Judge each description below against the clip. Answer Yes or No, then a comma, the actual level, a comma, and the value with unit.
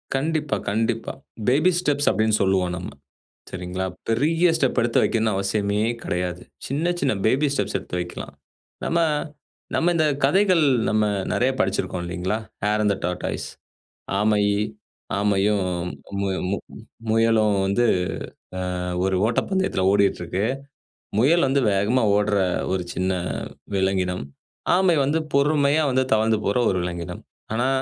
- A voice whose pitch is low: Yes, low, 110 Hz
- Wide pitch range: Yes, wide, 6.4 semitones